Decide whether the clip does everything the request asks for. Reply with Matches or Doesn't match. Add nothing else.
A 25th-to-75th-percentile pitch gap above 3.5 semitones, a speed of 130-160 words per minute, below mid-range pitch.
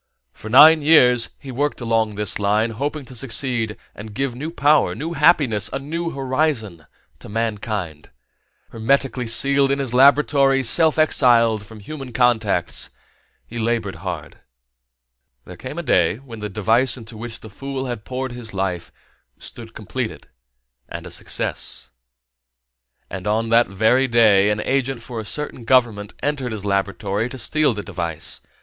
Matches